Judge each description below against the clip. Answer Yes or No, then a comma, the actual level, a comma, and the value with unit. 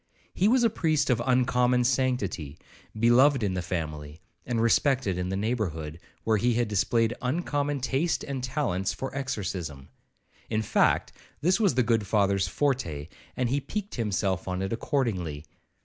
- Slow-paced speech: No, average, 150 wpm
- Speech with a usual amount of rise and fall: No, wide, 6.2 semitones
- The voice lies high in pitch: No, low, 115 Hz